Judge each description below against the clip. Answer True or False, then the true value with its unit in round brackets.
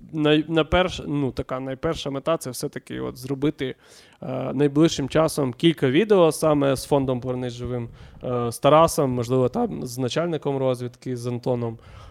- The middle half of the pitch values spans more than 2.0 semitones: True (3.5 semitones)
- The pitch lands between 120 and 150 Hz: True (135 Hz)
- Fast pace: False (145 wpm)